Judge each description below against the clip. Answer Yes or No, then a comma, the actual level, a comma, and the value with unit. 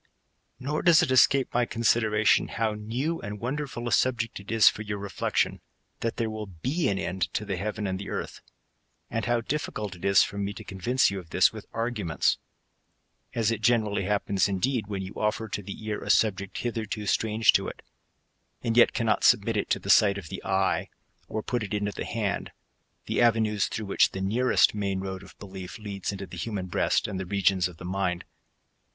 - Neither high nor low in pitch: No, low, 105 Hz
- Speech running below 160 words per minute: No, fast, 205 wpm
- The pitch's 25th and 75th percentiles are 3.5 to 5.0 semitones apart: No, average, 3.0 semitones